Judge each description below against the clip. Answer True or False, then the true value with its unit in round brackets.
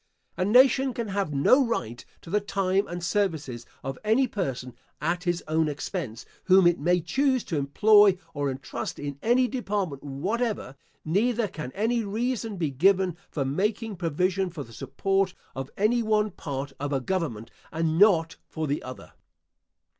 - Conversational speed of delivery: True (160 wpm)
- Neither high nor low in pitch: True (180 Hz)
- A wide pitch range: True (6.5 semitones)